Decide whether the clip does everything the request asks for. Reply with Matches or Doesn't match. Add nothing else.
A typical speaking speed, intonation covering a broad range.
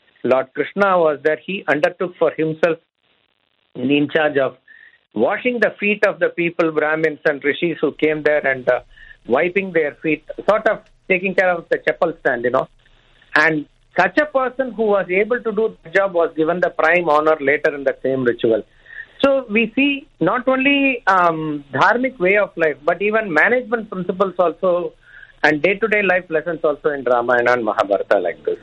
Matches